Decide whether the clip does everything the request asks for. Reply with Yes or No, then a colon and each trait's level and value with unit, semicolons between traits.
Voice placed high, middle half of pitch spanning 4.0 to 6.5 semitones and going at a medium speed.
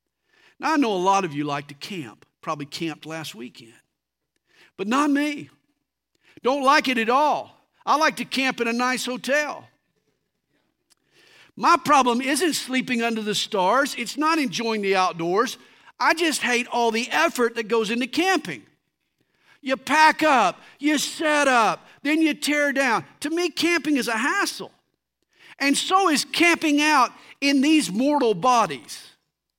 Yes: very high, 265 Hz; average, 5.0 semitones; average, 155 wpm